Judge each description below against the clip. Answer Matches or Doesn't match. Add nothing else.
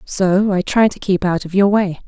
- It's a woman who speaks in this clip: Matches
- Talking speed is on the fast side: Matches